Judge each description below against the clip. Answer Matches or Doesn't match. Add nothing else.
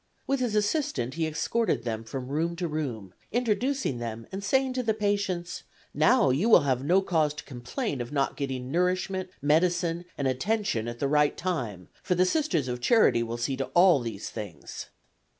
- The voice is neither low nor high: Matches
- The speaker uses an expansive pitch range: Matches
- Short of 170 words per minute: Doesn't match